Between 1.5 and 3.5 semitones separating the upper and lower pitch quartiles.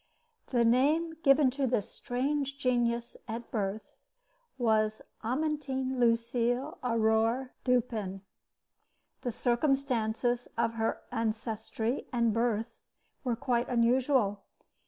Yes: narrow, 2.4 semitones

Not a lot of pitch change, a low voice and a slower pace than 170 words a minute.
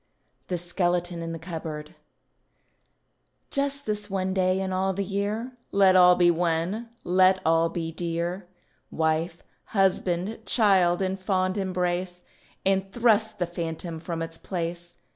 No: narrow, 2.3 semitones; medium, 180 Hz; slow, 135 wpm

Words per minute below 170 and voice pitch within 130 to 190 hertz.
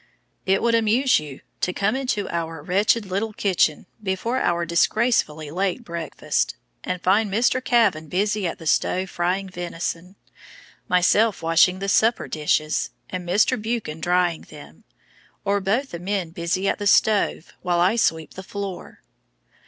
Yes: average, 150 wpm; medium, 185 Hz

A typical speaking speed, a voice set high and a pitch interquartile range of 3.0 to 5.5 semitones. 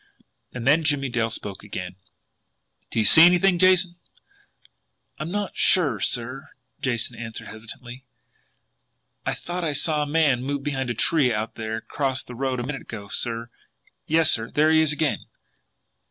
No: average, 160 wpm; low, 135 Hz; average, 5.2 semitones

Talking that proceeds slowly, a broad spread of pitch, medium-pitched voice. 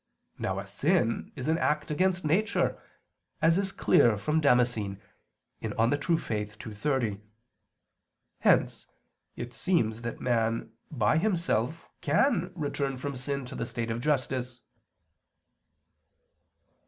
No: slow, 120 wpm; wide, 5.7 semitones; low, 130 Hz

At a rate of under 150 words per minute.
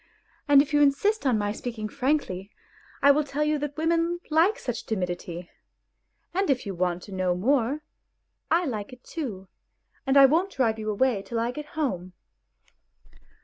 No: average, 170 wpm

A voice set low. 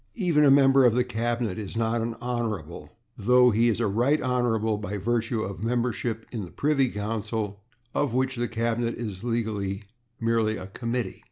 Yes: low, 115 Hz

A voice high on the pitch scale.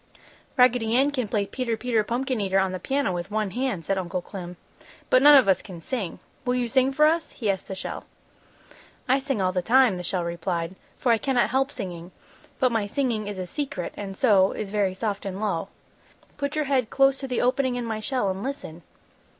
Yes: high, 220 Hz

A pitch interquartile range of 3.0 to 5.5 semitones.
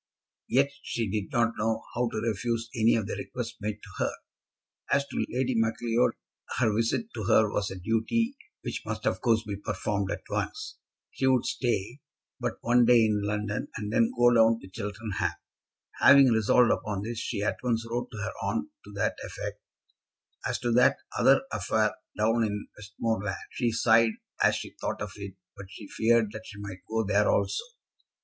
No: narrow, 2.4 semitones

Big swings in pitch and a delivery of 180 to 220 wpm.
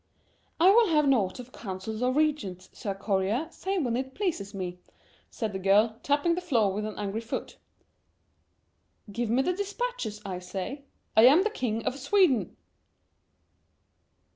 No: wide, 7.3 semitones; average, 155 wpm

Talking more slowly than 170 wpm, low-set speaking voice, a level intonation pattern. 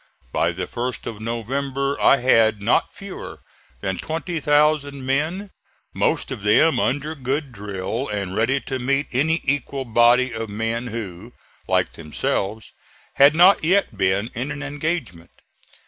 No: average, 140 wpm; low, 130 Hz; average, 4.8 semitones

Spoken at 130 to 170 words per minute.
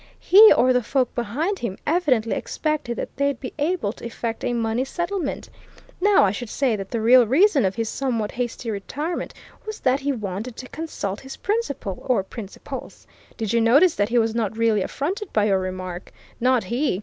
No: average, 190 wpm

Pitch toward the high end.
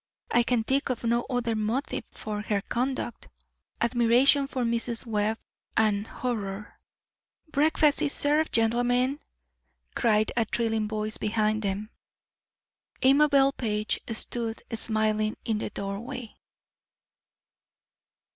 Yes: high, 230 Hz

